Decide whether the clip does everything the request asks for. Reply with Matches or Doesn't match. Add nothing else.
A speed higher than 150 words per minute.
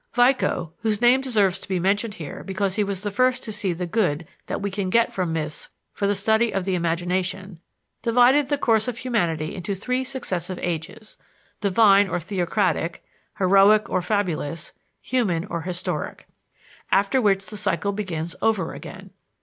Matches